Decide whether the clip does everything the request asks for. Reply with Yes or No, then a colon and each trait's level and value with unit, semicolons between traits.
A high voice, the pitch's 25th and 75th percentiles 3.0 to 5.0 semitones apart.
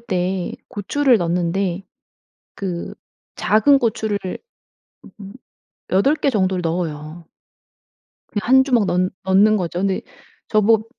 Yes: high, 195 Hz; average, 3.5 semitones